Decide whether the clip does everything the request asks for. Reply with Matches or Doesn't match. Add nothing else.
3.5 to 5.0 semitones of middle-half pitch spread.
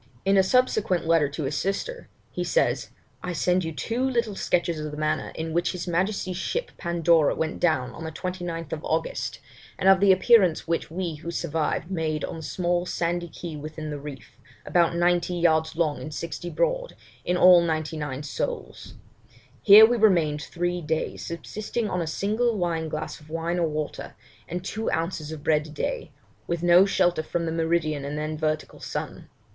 Doesn't match